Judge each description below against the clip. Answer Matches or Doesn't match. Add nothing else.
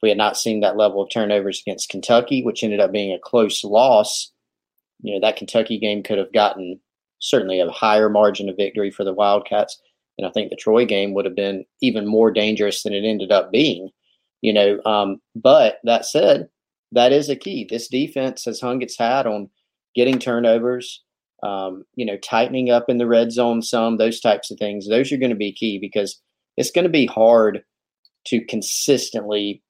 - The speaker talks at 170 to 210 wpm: Matches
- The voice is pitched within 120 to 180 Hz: Doesn't match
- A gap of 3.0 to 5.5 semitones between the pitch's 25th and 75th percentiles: Doesn't match